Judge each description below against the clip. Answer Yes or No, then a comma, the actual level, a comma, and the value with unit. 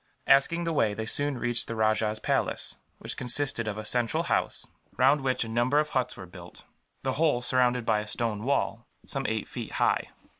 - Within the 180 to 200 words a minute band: Yes, average, 195 wpm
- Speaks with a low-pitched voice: Yes, low, 120 Hz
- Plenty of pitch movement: No, average, 3.8 semitones